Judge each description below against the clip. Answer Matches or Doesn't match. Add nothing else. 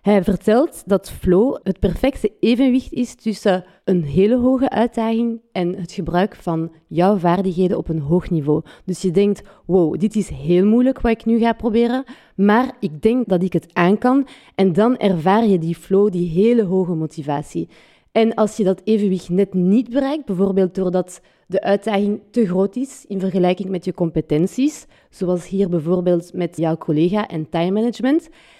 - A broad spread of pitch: Doesn't match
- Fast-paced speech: Doesn't match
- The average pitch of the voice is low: Doesn't match